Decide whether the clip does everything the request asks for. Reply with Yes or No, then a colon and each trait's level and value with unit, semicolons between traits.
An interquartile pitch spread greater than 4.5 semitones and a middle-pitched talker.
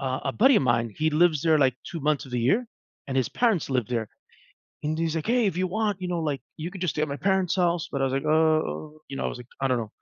Yes: average, 4.9 semitones; medium, 155 Hz